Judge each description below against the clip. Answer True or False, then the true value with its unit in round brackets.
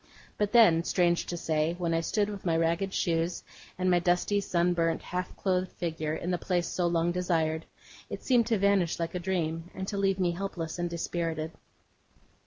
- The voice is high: False (175 Hz)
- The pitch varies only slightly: True (2.2 semitones)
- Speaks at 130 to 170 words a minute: False (190 wpm)